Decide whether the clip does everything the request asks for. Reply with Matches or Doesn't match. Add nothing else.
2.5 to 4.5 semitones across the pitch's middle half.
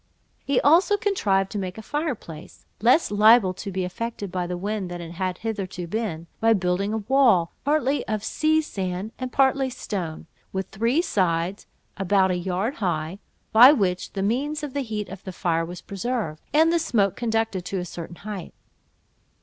Doesn't match